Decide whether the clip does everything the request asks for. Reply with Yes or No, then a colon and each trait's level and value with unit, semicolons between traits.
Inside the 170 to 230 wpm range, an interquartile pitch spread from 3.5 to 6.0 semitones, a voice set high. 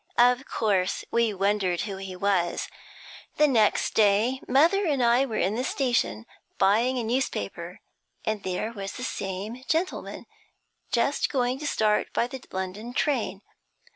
No: average, 145 wpm; average, 4.6 semitones; high, 225 Hz